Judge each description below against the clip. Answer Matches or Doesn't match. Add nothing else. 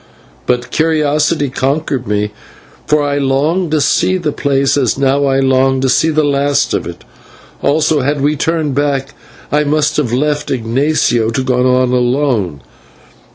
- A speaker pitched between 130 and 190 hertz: Matches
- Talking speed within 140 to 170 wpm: Matches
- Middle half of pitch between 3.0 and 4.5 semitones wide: Doesn't match